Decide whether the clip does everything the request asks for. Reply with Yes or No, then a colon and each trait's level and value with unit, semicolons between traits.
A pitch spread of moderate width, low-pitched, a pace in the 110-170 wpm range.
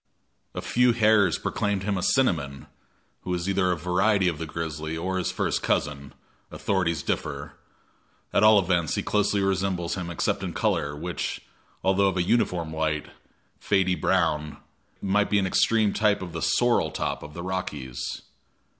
Yes: average, 3.5 semitones; very low, 90 Hz; average, 165 wpm